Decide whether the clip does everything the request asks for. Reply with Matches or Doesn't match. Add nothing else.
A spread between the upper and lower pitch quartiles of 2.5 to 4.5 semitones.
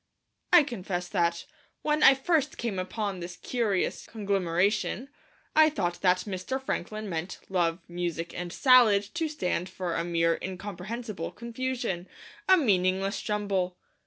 Doesn't match